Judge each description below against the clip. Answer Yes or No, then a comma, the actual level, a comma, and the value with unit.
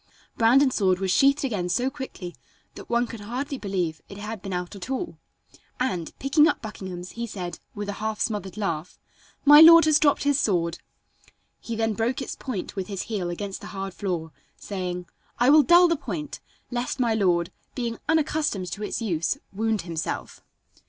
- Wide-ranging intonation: Yes, wide, 6.2 semitones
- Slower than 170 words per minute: No, average, 180 wpm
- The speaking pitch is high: Yes, high, 215 Hz